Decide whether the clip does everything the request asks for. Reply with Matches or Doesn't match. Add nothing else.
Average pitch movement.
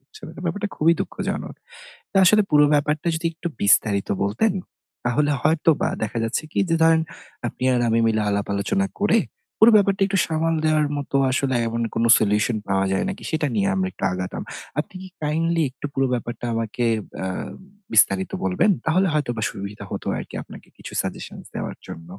Doesn't match